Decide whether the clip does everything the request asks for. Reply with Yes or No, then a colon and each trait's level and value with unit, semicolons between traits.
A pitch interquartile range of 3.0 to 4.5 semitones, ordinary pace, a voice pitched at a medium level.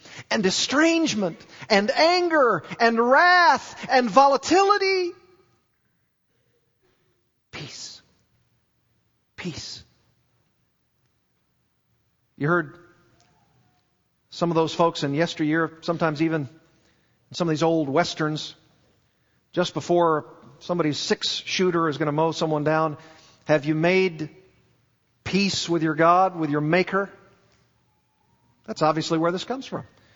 No: average, 3.7 semitones; slow, 105 wpm; medium, 165 Hz